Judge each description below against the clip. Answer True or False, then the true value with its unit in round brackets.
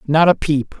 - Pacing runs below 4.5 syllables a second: False (4.6 syllables/s)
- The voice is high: False (150 Hz)